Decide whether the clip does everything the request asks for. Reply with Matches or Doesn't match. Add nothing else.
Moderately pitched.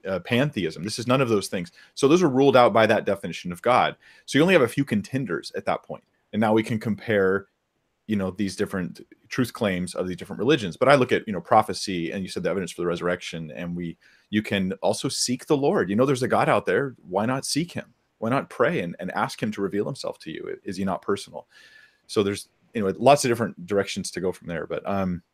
Doesn't match